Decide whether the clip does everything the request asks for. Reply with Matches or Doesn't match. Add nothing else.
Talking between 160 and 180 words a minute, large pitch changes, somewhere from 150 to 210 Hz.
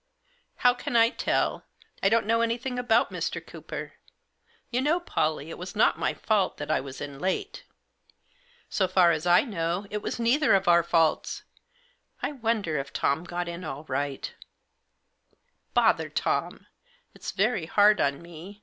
Matches